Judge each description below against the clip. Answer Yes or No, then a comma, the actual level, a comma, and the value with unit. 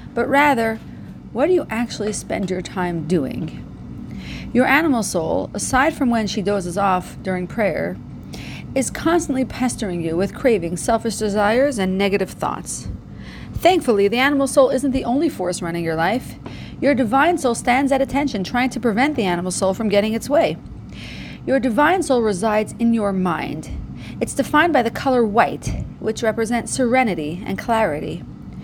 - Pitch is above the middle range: Yes, high, 230 Hz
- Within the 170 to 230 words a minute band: No, average, 160 wpm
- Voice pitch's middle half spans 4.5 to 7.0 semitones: Yes, average, 5.2 semitones